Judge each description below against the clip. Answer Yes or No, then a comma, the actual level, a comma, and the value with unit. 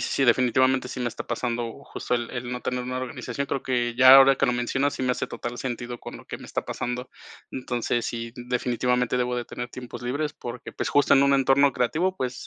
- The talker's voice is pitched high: No, low, 125 Hz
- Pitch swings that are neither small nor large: No, narrow, 1.5 semitones